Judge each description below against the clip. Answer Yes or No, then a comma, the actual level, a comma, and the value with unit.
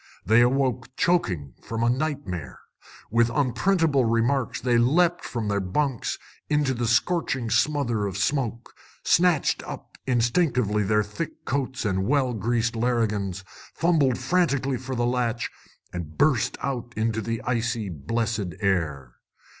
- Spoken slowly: Yes, slow, 130 wpm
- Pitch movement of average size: Yes, average, 4.2 semitones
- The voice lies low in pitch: Yes, low, 120 Hz